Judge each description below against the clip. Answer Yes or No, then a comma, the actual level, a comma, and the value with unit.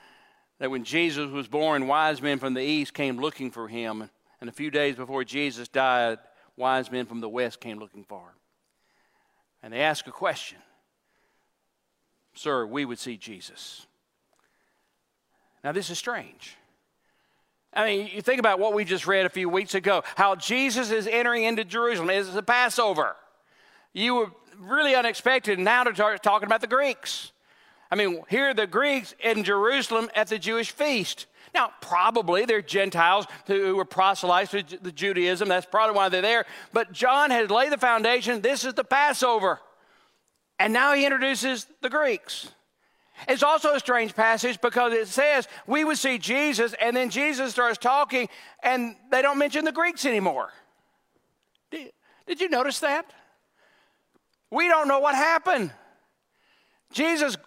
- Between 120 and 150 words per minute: No, average, 160 wpm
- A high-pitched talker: Yes, high, 225 Hz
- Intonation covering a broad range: Yes, wide, 6.6 semitones